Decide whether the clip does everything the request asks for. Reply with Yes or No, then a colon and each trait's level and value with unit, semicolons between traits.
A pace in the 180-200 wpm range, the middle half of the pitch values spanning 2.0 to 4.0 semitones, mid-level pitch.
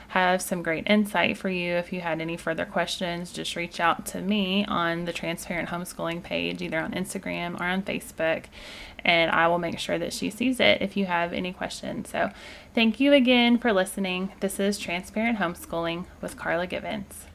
Yes: average, 190 wpm; average, 2.8 semitones; medium, 180 Hz